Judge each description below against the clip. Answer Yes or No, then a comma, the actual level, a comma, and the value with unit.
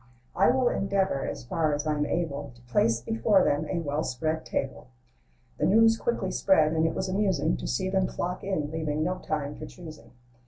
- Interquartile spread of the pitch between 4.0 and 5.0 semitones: Yes, average, 4.6 semitones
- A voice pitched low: No, medium, 160 Hz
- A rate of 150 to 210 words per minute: Yes, average, 195 wpm